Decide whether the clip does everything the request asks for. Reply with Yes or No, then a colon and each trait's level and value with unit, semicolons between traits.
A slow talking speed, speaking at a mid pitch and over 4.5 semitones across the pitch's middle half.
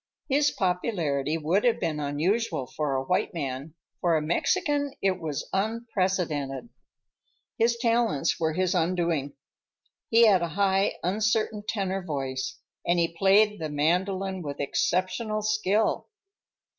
Yes: slow, 130 wpm; medium, 180 Hz; wide, 5.4 semitones